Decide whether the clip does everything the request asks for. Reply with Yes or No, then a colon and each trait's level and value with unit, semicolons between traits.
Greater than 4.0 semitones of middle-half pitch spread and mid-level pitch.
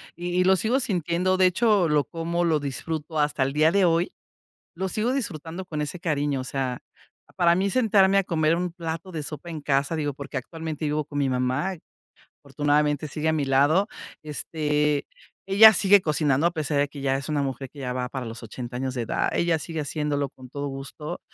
No: average, 3.6 semitones; medium, 155 Hz